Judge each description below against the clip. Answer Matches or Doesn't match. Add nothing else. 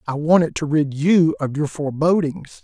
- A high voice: Doesn't match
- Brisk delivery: Doesn't match